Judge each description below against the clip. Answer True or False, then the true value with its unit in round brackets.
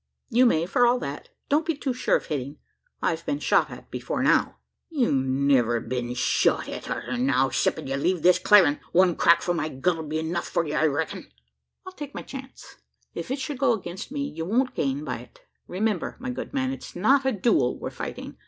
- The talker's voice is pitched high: False (180 Hz)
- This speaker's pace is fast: True (210 wpm)